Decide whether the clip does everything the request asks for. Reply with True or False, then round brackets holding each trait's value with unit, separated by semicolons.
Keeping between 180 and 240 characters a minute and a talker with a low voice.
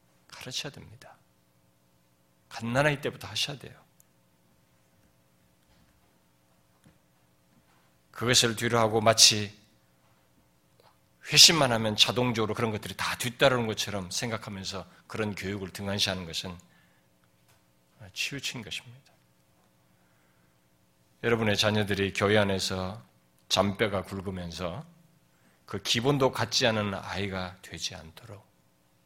True (230 characters per minute; 90 Hz)